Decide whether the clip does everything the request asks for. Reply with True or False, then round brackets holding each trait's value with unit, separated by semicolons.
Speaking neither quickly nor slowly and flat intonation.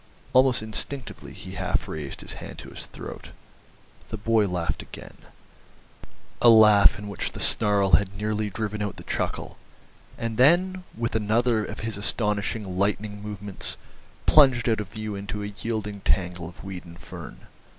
True (160 wpm; 2.2 semitones)